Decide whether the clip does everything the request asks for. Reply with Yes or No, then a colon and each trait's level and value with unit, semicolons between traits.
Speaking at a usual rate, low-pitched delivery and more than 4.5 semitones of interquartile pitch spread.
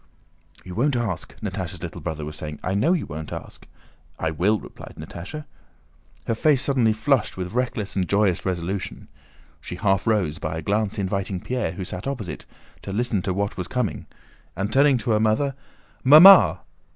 Yes: average, 175 wpm; low, 100 Hz; wide, 5.4 semitones